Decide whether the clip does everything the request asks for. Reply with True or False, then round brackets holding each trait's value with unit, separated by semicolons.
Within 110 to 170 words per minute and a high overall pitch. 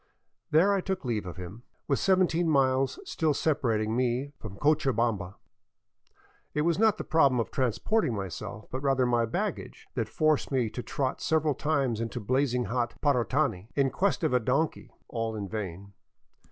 False (165 wpm; 130 Hz)